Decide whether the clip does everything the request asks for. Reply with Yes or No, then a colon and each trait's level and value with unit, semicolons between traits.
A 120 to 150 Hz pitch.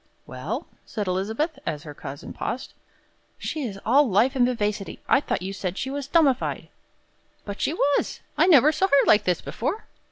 No: high, 245 Hz